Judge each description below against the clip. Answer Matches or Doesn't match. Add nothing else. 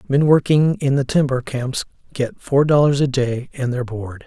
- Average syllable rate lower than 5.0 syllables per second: Matches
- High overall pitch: Doesn't match